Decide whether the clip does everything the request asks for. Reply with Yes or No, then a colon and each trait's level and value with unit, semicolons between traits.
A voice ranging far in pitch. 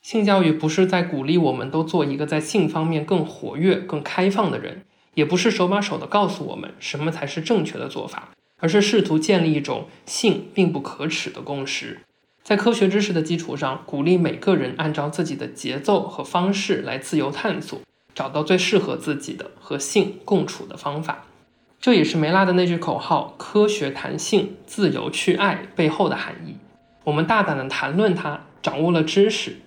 No: average, 4.4 semitones